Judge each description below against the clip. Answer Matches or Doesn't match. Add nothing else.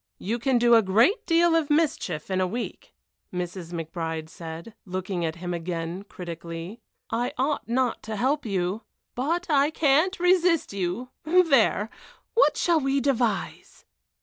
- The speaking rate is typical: Matches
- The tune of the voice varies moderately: Doesn't match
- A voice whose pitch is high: Matches